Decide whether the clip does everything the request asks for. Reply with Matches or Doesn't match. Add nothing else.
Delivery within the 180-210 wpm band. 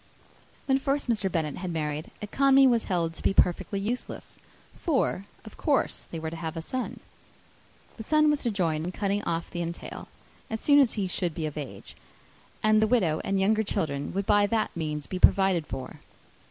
Matches